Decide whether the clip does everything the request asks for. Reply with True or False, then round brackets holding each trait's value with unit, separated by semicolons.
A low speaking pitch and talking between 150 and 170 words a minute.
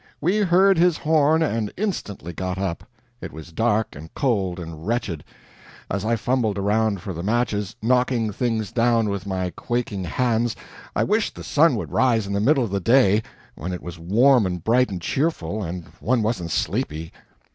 False (110 Hz; 180 wpm)